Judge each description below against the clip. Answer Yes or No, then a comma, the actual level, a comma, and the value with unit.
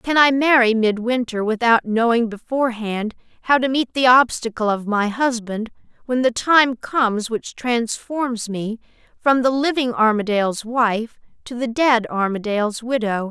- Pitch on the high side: Yes, high, 235 Hz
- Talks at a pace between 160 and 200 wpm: No, average, 145 wpm